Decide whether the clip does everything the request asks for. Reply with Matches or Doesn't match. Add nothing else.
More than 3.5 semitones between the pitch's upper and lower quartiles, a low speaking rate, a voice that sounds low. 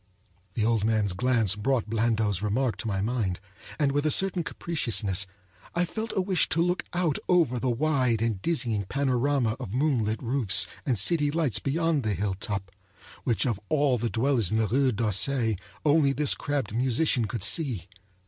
Doesn't match